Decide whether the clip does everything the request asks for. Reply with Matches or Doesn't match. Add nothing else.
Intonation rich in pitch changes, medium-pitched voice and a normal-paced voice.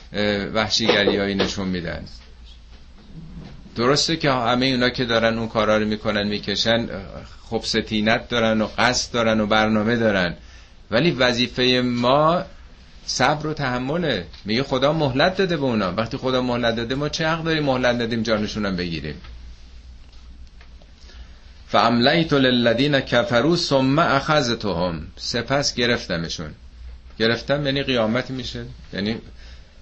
Doesn't match